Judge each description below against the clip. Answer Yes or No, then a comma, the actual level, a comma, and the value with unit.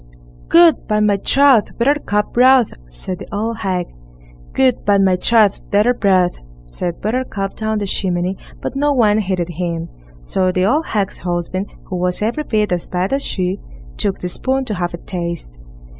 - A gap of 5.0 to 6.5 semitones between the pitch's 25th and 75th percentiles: No, average, 4.2 semitones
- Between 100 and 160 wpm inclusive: No, average, 175 wpm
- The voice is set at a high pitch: Yes, high, 200 Hz